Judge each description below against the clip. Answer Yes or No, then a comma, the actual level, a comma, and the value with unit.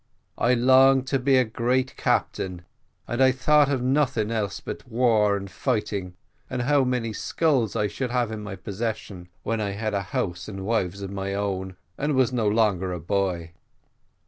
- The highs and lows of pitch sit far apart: No, average, 4.6 semitones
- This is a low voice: Yes, low, 110 Hz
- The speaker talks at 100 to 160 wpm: No, average, 185 wpm